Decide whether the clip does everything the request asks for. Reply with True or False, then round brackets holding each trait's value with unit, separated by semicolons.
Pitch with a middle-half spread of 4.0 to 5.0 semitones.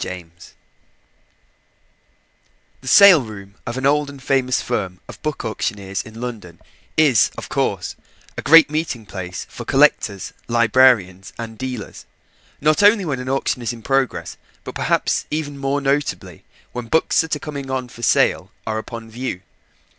True (4.5 semitones)